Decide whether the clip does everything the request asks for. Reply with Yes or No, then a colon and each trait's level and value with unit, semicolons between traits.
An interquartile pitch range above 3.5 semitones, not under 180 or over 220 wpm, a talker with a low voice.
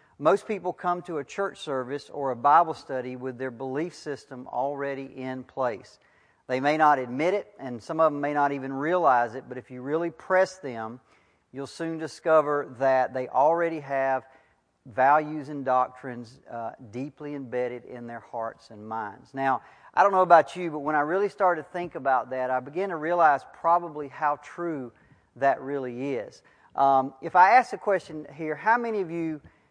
No: average, 4.2 semitones; average, 185 wpm; medium, 145 Hz